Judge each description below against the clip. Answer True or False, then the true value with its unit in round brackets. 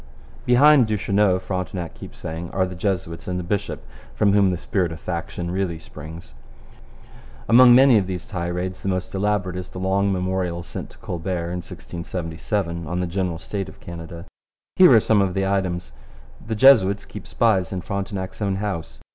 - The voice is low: True (95 Hz)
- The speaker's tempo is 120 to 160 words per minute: False (175 wpm)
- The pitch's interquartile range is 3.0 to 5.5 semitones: False (2.5 semitones)